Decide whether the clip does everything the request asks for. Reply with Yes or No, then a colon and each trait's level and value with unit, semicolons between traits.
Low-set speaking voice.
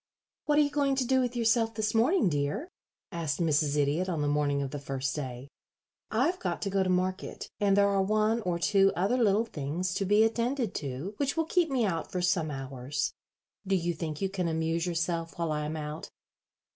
No: medium, 185 Hz